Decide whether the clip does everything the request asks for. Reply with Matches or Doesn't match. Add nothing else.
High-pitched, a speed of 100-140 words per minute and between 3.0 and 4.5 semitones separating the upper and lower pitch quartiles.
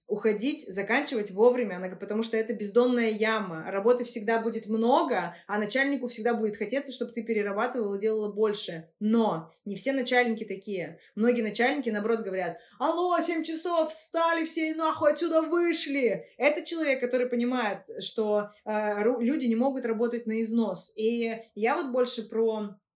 Doesn't match